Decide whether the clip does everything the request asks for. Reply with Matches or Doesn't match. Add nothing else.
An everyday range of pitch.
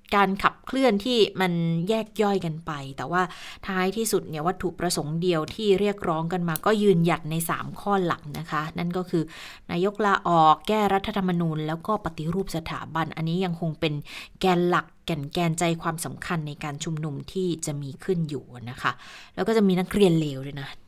Matches